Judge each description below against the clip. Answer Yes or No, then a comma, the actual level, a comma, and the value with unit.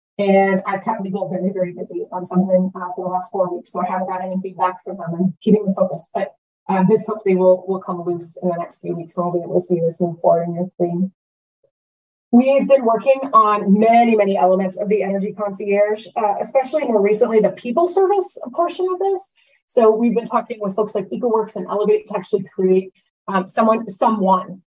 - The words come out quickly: Yes, fast, 220 wpm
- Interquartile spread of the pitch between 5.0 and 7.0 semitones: No, average, 3.2 semitones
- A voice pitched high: Yes, high, 195 Hz